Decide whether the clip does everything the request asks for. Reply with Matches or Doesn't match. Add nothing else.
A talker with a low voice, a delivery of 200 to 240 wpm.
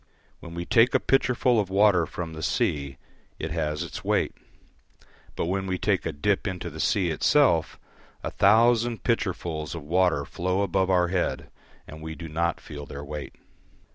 Doesn't match